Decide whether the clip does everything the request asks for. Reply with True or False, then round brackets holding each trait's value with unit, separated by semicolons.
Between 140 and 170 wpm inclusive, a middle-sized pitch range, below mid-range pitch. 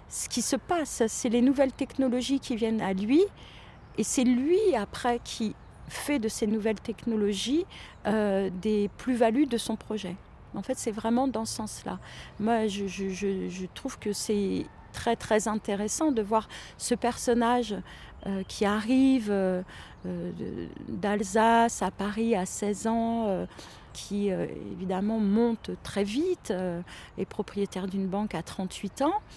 False (150 wpm; 3.3 semitones; 220 Hz)